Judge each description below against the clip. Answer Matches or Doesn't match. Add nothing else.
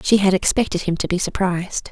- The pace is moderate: Doesn't match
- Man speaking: Doesn't match